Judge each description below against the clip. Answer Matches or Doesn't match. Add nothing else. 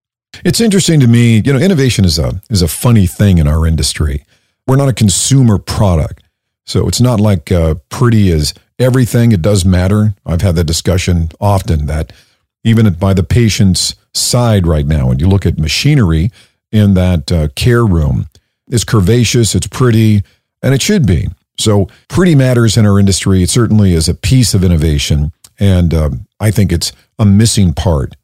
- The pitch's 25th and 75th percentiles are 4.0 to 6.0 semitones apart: Matches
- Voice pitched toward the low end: Matches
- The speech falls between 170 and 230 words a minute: Matches